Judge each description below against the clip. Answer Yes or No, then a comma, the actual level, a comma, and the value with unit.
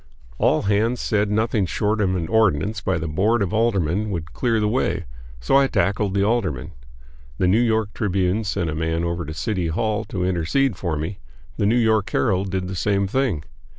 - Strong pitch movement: No, average, 3.9 semitones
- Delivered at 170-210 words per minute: Yes, average, 200 wpm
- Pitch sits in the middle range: No, low, 100 Hz